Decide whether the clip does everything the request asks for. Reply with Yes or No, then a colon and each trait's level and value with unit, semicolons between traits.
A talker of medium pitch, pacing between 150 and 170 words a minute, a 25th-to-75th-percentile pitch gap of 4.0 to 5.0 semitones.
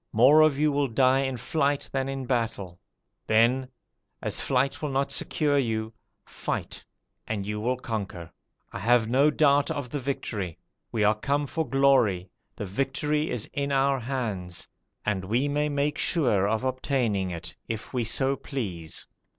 No: low, 130 Hz; average, 165 wpm; average, 4.4 semitones